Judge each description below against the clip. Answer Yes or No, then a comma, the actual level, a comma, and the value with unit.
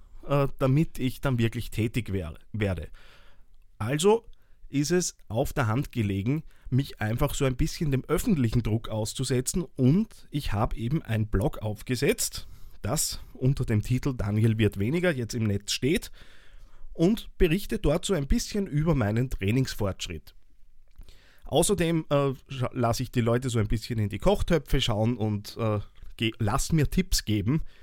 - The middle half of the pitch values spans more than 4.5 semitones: Yes, average, 5.1 semitones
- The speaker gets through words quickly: No, average, 140 wpm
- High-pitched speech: No, low, 125 Hz